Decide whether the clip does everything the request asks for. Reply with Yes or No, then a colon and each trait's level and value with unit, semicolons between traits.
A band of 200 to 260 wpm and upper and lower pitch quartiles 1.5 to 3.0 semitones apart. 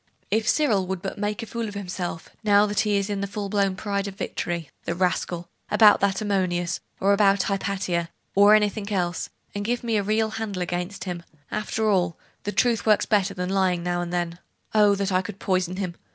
Yes: fast, 205 wpm; narrow, 2.5 semitones